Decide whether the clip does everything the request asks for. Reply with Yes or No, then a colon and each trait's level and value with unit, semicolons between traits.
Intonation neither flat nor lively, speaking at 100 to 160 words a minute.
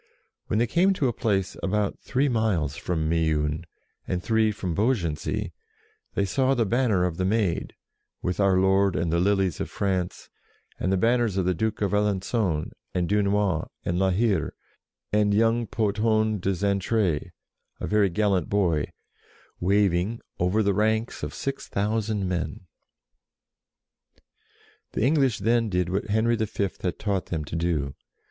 Yes: average, 3.5 semitones; average, 150 wpm